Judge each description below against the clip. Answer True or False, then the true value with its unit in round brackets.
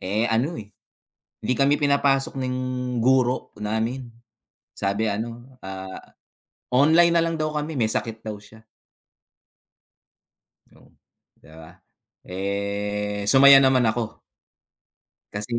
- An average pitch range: True (4.7 semitones)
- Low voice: True (115 Hz)